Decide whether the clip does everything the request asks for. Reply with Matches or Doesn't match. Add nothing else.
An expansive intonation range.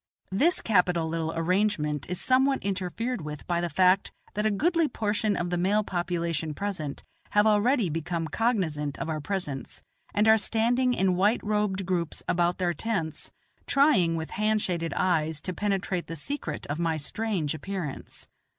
Doesn't match